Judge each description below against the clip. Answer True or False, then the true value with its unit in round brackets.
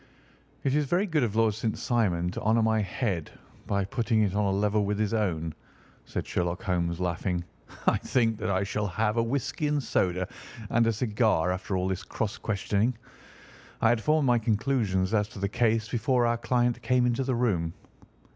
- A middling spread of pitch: True (3.9 semitones)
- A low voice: True (110 Hz)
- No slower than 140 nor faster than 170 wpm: False (195 wpm)